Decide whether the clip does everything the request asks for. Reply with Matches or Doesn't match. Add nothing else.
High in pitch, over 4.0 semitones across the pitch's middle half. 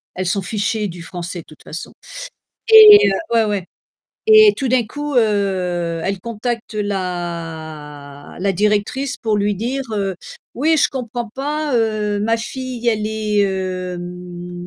Matches